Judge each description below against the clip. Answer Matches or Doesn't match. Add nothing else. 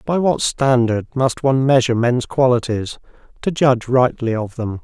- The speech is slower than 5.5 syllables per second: Matches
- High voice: Doesn't match